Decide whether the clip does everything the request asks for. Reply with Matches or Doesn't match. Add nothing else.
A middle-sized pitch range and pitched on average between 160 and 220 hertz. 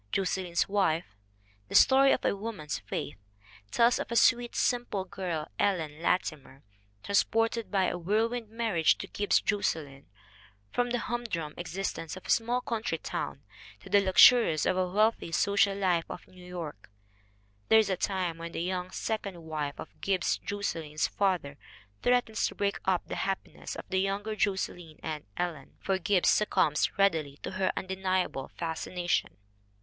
Matches